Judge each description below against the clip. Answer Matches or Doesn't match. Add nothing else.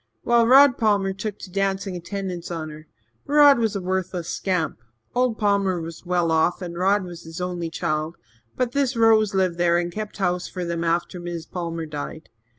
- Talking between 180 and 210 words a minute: Matches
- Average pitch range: Matches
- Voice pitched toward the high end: Doesn't match